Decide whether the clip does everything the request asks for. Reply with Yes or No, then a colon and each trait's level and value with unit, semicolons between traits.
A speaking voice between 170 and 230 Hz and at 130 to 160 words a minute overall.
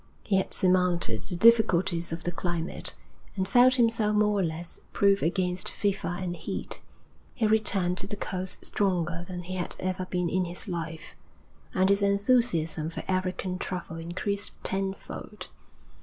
Yes: medium, 185 Hz; average, 155 wpm